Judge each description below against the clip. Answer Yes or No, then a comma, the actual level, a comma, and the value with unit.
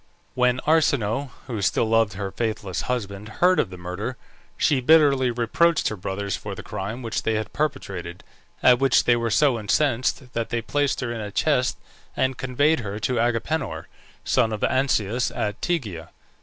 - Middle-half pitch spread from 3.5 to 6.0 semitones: Yes, average, 4.0 semitones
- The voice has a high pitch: No, low, 120 Hz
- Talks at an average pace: Yes, average, 170 wpm